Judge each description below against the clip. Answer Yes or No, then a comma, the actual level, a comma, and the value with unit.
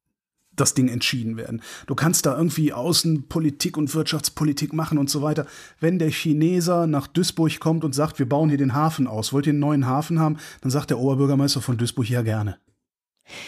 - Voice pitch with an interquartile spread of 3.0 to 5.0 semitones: No, narrow, 2.6 semitones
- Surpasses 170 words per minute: Yes, fast, 190 wpm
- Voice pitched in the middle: Yes, medium, 150 Hz